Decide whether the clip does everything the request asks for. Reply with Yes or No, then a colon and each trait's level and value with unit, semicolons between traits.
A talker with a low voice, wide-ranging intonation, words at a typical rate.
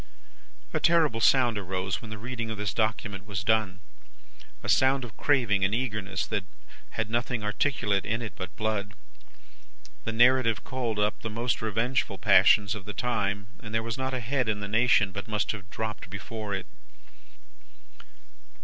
No: low, 110 Hz; average, 2.7 semitones; average, 165 wpm